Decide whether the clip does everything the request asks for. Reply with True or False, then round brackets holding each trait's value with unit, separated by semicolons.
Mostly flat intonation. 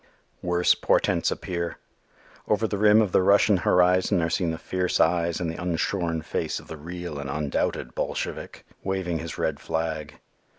True (2.3 semitones)